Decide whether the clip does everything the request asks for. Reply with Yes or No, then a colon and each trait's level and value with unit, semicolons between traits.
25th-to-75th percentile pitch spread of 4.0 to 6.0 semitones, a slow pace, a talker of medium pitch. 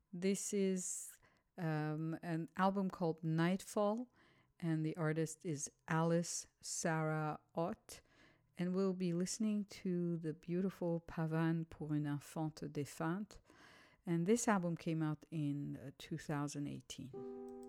No: average, 3.1 semitones; slow, 115 wpm; medium, 165 Hz